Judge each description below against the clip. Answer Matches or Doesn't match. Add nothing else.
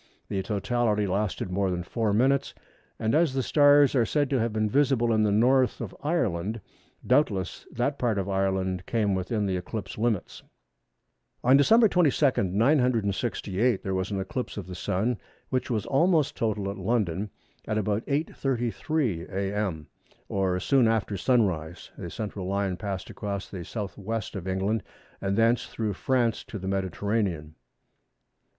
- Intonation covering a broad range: Doesn't match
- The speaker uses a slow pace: Doesn't match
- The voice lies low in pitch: Matches